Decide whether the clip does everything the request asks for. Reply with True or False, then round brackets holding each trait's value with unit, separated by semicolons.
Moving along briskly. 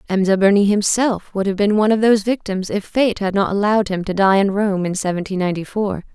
True (245 wpm)